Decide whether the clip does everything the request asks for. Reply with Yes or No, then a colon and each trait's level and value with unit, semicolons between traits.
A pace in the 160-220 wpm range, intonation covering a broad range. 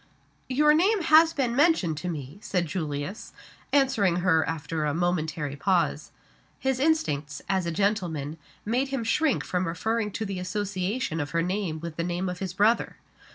Yes: average, 165 wpm; wide, 6.4 semitones